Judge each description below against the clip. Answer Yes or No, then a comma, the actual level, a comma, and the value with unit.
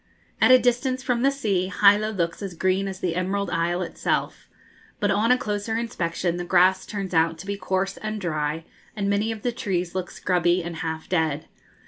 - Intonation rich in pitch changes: No, average, 3.5 semitones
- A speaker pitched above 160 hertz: Yes, high, 190 Hz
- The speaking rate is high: No, average, 195 wpm